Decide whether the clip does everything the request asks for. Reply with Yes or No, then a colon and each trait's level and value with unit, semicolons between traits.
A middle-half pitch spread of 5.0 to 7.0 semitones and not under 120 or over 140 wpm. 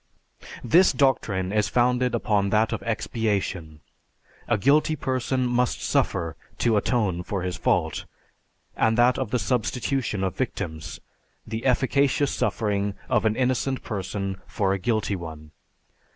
No: average, 4.3 semitones; slow, 135 wpm